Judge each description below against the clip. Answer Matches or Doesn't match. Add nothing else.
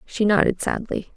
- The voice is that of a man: Doesn't match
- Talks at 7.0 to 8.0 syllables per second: Doesn't match